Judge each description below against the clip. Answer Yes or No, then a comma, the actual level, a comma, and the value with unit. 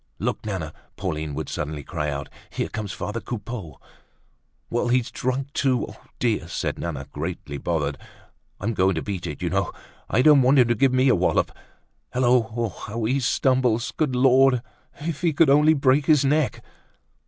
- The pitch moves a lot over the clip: Yes, wide, 6.6 semitones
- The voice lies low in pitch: Yes, low, 120 Hz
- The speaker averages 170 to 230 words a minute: Yes, average, 175 wpm